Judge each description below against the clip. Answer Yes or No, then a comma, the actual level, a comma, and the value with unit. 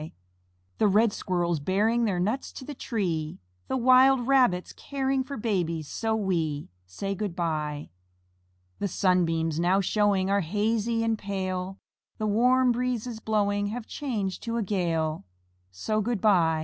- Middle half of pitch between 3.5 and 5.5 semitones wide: Yes, average, 4.7 semitones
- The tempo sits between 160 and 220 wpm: No, average, 145 wpm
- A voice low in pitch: No, high, 205 Hz